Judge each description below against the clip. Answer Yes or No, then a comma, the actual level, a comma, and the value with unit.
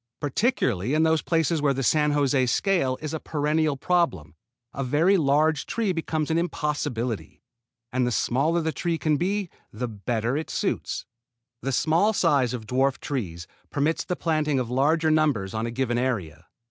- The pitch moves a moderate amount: Yes, average, 4.3 semitones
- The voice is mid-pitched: Yes, medium, 145 Hz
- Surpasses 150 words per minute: Yes, average, 170 wpm